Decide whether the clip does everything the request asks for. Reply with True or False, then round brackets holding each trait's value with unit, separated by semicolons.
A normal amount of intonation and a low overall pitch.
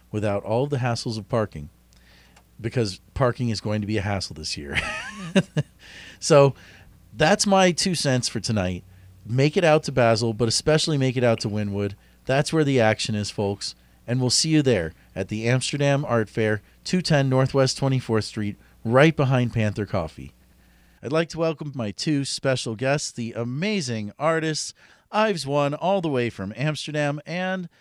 False (6.1 semitones; 120 Hz)